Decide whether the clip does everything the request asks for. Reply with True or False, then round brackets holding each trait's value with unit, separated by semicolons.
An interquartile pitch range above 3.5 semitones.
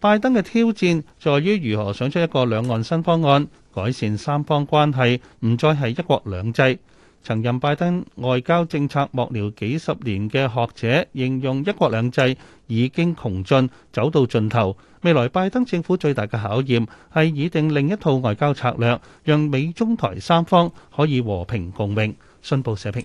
True (5.5 semitones)